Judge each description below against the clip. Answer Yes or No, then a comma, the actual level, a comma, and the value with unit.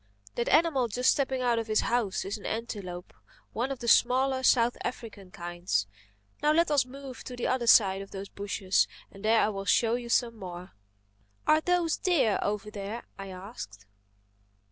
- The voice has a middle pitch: No, high, 230 Hz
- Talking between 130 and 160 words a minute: No, average, 180 wpm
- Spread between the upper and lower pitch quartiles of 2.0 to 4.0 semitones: No, average, 4.5 semitones